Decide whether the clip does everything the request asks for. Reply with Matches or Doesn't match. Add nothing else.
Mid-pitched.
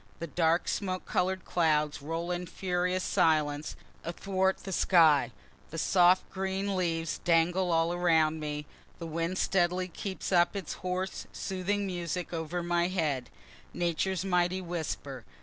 Matches